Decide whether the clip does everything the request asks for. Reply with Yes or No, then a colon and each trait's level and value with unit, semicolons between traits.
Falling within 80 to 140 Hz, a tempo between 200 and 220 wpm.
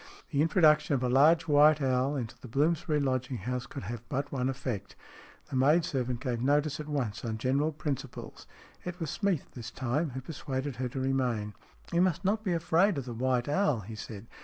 Yes: low, 135 Hz; fast, 205 wpm